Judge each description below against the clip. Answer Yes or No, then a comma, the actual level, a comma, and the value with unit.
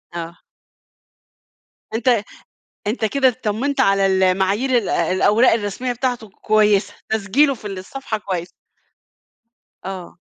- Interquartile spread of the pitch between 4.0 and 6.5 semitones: Yes, average, 4.3 semitones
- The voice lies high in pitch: Yes, high, 210 Hz